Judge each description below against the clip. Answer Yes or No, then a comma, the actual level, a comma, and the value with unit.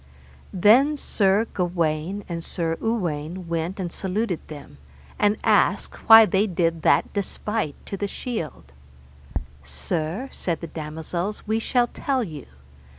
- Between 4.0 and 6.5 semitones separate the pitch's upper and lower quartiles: Yes, average, 4.6 semitones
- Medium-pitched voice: Yes, medium, 180 Hz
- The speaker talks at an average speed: No, slow, 130 wpm